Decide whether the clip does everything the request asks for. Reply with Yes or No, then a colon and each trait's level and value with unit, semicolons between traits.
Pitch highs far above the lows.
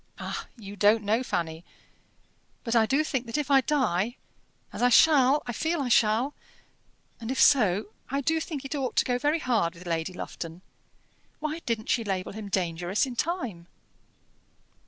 Yes: wide, 6.0 semitones